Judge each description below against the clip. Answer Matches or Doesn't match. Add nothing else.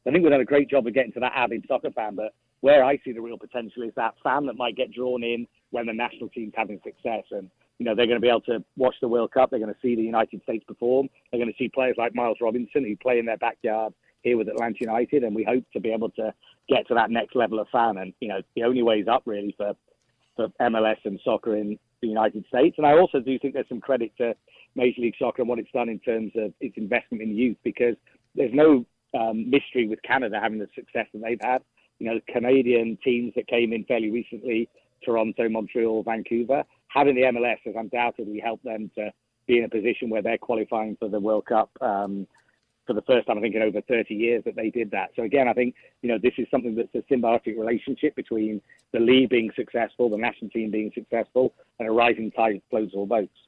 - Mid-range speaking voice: Doesn't match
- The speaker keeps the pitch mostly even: Matches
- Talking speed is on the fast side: Matches